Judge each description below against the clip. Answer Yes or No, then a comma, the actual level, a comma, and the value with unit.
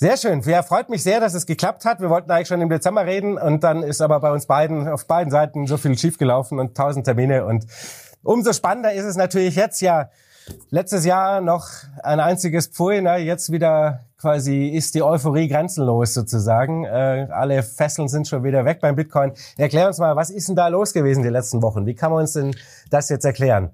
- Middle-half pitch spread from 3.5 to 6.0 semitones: Yes, average, 4.3 semitones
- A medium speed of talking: No, fast, 215 wpm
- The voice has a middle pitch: Yes, medium, 155 Hz